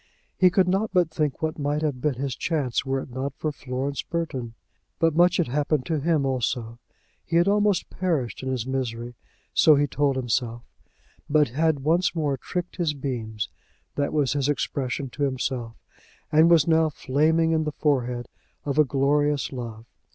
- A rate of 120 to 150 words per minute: No, average, 175 wpm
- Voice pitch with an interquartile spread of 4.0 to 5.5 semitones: No, average, 3.6 semitones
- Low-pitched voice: No, medium, 145 Hz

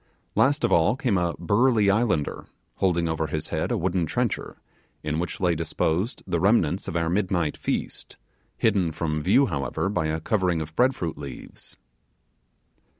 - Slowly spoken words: No, average, 160 wpm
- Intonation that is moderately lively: Yes, average, 4.1 semitones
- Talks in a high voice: No, very low, 85 Hz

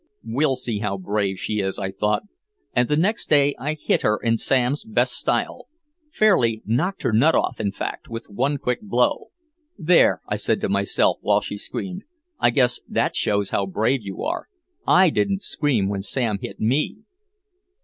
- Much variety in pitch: Yes, wide, 6.5 semitones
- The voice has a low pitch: Yes, low, 120 Hz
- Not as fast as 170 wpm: No, average, 180 wpm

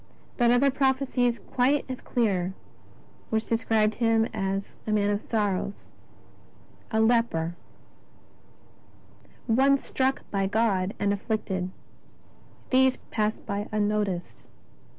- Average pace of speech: No, slow, 110 wpm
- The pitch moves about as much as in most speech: Yes, average, 3.3 semitones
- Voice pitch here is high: Yes, high, 220 Hz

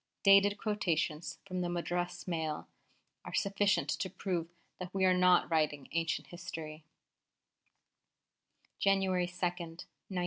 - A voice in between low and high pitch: Yes, medium, 175 Hz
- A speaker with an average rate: No, slow, 115 wpm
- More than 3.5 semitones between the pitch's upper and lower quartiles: No, narrow, 2.5 semitones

